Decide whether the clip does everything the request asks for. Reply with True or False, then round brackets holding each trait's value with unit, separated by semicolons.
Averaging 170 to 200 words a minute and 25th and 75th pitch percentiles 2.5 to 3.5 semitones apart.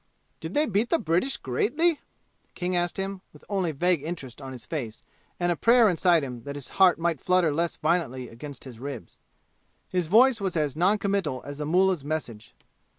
False (190 wpm; 5.2 semitones)